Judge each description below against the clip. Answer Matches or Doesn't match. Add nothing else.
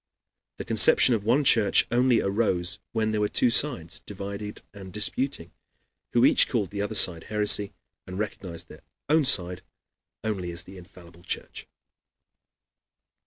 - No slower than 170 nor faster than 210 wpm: Doesn't match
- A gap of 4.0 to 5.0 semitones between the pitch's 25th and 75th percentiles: Doesn't match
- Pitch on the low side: Matches